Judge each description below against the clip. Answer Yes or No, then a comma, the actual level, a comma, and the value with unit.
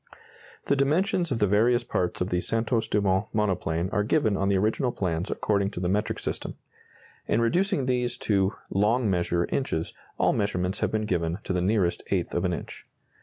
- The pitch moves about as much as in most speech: Yes, average, 4.5 semitones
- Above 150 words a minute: Yes, average, 185 wpm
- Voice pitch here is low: Yes, low, 105 Hz